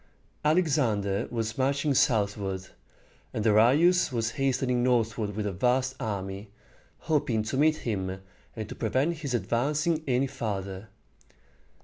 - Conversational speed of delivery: No, slow, 120 wpm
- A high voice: No, low, 120 Hz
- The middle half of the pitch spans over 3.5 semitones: Yes, average, 4.7 semitones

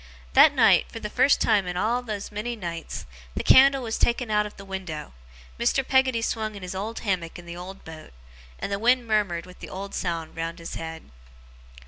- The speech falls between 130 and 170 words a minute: No, fast, 205 wpm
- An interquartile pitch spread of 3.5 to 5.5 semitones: Yes, average, 4.7 semitones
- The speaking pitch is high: Yes, high, 200 Hz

